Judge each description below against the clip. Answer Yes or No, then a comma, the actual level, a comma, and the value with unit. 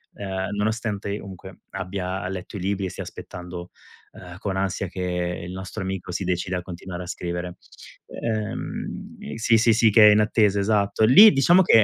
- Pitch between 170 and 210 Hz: No, very low, 95 Hz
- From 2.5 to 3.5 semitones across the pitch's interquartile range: Yes, average, 2.8 semitones